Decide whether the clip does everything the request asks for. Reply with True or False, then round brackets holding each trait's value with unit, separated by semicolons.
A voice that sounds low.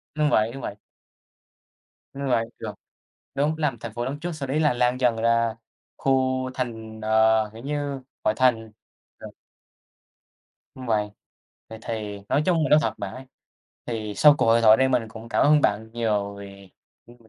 True (115 Hz)